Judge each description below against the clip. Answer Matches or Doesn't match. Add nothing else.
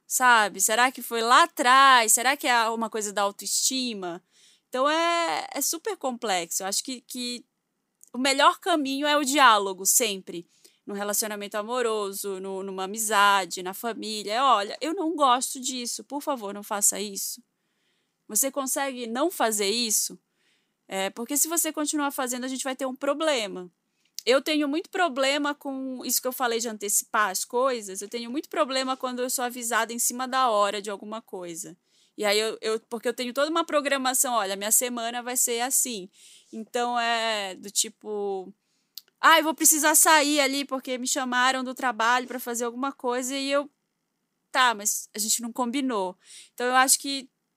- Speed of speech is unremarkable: Matches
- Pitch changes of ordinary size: Matches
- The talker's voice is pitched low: Doesn't match